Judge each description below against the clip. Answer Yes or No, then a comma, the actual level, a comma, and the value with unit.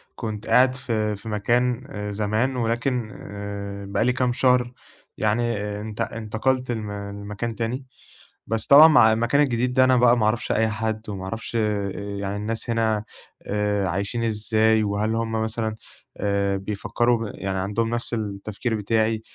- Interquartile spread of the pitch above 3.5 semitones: No, narrow, 2.5 semitones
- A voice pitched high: No, low, 110 Hz